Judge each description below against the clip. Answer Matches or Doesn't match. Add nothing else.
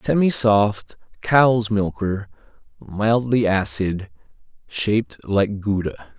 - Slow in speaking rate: Matches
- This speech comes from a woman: Doesn't match